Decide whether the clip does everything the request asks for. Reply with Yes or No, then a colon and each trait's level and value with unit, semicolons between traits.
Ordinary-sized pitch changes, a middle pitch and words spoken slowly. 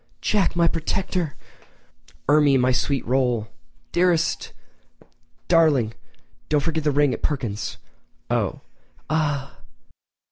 Yes: average, 4.1 semitones; medium, 145 Hz; slow, 100 wpm